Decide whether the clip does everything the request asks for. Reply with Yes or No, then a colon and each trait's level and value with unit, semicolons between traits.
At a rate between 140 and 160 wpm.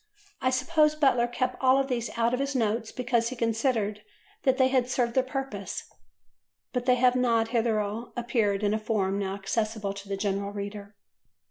No: average, 175 wpm